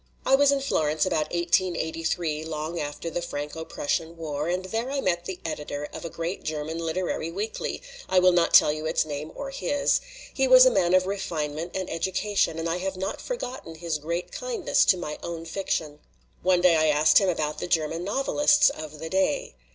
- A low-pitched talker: No, medium, 170 Hz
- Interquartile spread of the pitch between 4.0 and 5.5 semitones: No, average, 3.3 semitones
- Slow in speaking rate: No, average, 200 wpm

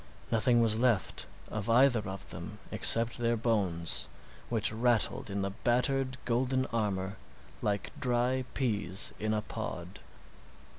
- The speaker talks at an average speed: No, slow, 130 wpm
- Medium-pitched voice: No, low, 115 Hz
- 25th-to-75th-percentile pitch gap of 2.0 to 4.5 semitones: Yes, average, 3.3 semitones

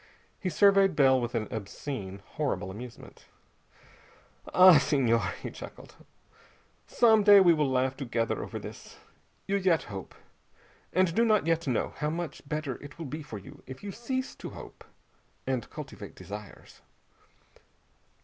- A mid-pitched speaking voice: Yes, medium, 145 Hz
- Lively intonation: Yes, wide, 7.3 semitones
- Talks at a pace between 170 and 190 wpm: No, average, 145 wpm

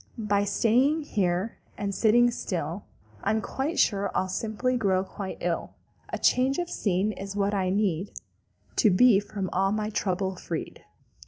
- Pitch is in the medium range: No, high, 200 Hz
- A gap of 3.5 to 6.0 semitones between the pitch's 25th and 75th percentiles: No, average, 2.7 semitones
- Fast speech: No, average, 150 wpm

